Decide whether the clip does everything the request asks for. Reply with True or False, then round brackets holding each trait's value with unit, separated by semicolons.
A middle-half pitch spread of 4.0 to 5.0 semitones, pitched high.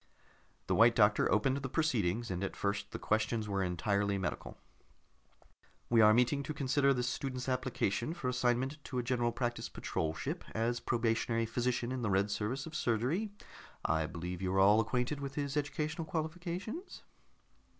False (4.6 semitones; 120 Hz)